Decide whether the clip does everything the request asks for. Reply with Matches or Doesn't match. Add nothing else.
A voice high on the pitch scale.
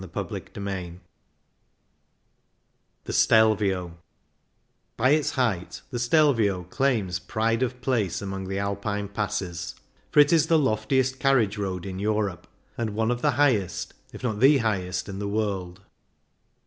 Doesn't match